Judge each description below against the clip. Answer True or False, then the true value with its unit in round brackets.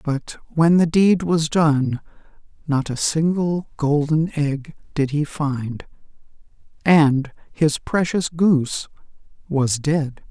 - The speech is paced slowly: True (115 wpm)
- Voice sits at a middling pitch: True (150 Hz)